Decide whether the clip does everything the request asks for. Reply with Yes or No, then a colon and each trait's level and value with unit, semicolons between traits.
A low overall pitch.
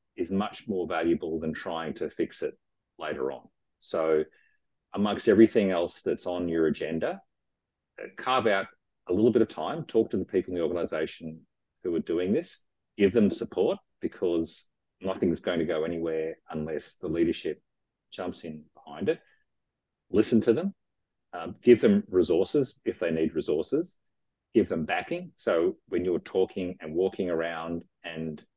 Yes: very low, 95 Hz